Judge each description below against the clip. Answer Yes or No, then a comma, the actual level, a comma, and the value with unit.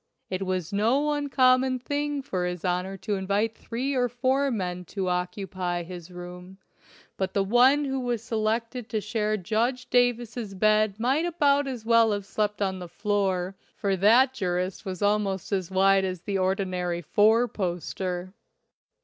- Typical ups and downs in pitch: Yes, average, 4.7 semitones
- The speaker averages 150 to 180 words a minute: Yes, average, 160 wpm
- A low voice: No, high, 205 Hz